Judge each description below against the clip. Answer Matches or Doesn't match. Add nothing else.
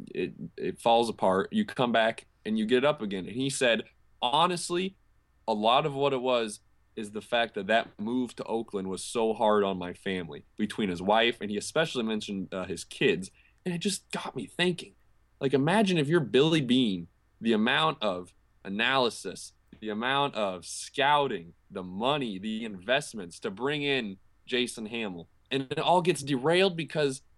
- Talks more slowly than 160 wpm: Doesn't match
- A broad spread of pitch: Matches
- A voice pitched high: Doesn't match